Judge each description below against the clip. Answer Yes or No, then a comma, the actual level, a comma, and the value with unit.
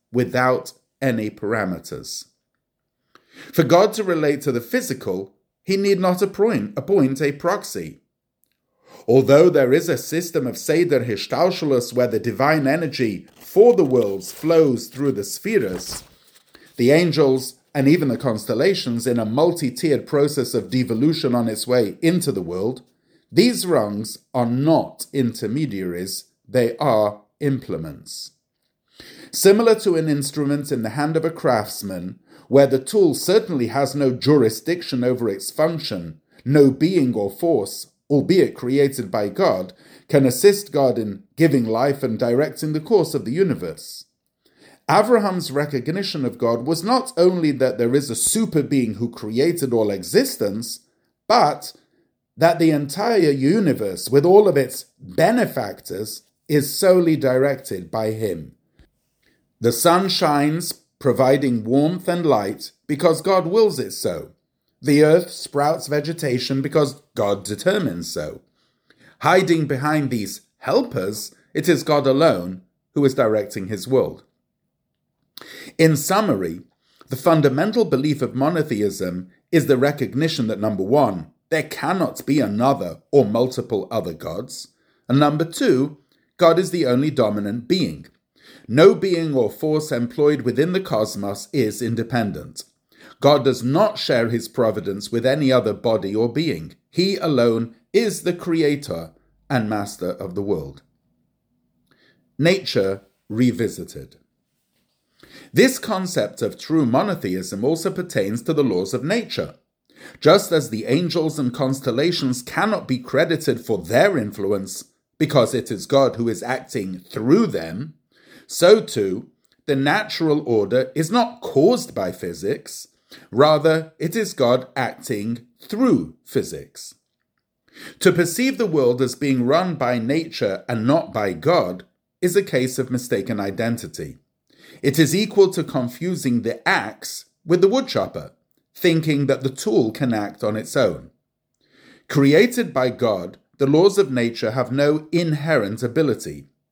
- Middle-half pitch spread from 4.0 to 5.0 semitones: No, wide, 5.5 semitones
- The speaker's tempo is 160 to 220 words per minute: No, slow, 135 wpm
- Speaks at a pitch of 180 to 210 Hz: No, medium, 140 Hz